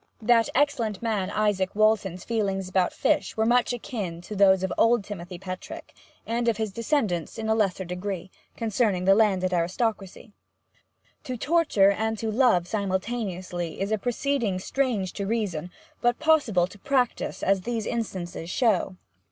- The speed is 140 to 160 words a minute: Yes, average, 150 wpm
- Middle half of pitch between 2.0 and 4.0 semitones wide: Yes, average, 3.7 semitones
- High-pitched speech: Yes, high, 205 Hz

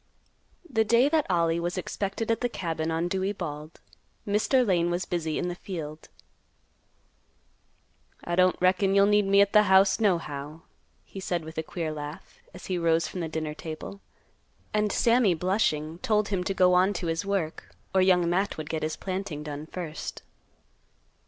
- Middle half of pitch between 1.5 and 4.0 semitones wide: Yes, average, 3.5 semitones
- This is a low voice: No, medium, 180 Hz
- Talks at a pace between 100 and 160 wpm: No, average, 175 wpm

